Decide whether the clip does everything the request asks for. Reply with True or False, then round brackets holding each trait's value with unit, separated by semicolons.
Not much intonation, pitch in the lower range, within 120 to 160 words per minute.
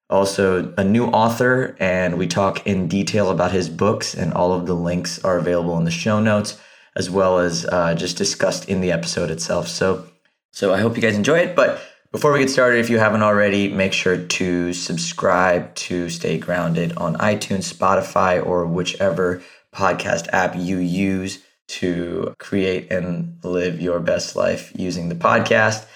False (2.1 semitones; 90 Hz; 175 wpm)